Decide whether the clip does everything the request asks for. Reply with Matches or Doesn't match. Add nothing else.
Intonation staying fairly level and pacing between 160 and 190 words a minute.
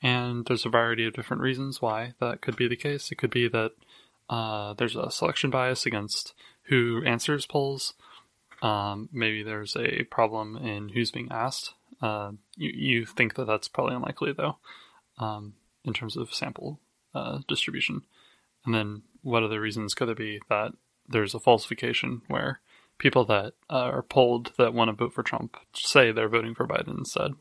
Matches